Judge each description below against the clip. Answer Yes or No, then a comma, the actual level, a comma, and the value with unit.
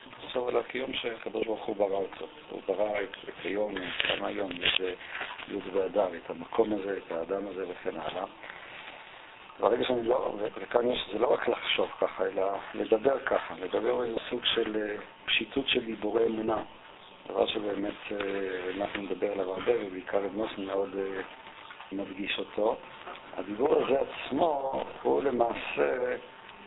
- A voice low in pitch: Yes, low, 105 Hz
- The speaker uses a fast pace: No, average, 140 wpm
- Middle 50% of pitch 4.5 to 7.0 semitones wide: No, narrow, 2.5 semitones